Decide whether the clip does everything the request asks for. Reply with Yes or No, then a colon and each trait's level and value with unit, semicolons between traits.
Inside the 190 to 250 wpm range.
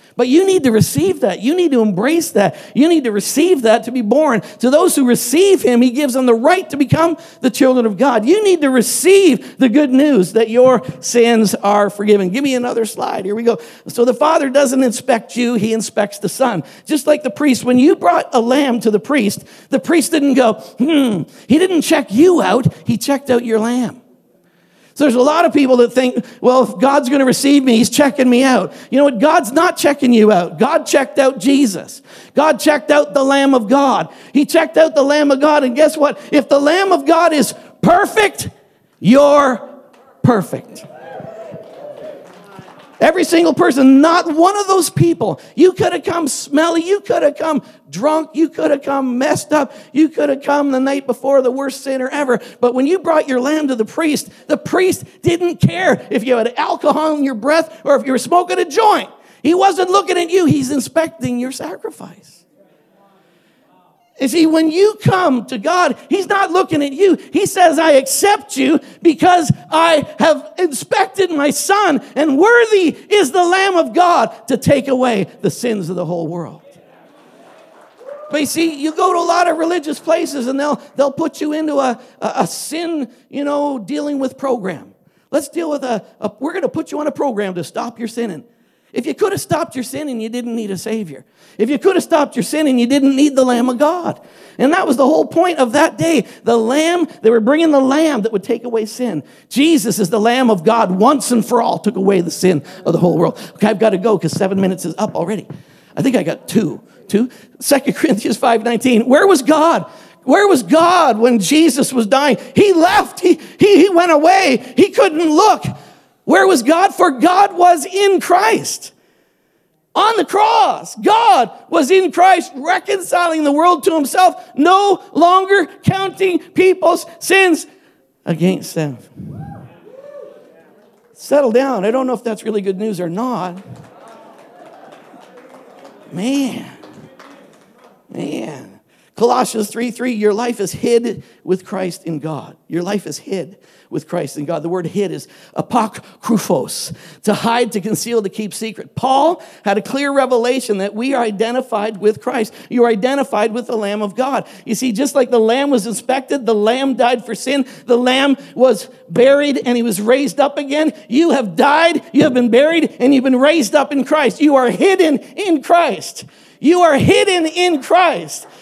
Yes: average, 195 wpm